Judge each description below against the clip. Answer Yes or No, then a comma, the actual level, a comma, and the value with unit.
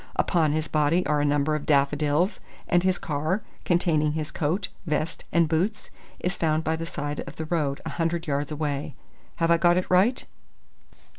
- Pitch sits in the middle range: Yes, medium, 160 Hz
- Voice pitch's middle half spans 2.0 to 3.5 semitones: Yes, average, 2.7 semitones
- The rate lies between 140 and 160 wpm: No, average, 180 wpm